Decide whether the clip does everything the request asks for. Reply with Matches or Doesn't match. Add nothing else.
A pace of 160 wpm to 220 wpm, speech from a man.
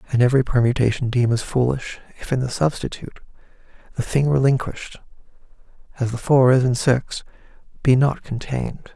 Doesn't match